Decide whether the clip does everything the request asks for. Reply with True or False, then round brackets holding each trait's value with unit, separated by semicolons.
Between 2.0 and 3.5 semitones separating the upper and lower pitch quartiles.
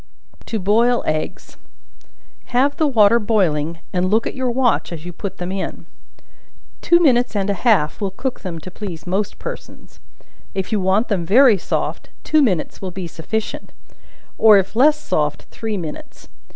False (4.8 semitones)